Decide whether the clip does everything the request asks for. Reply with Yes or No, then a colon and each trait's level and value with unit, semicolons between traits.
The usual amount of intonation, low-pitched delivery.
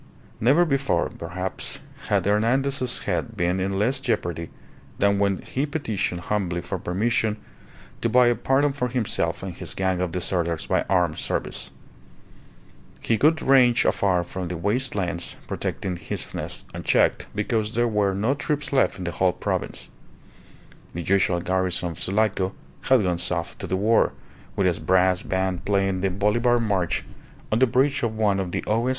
Yes: average, 4.7 semitones; low, 100 Hz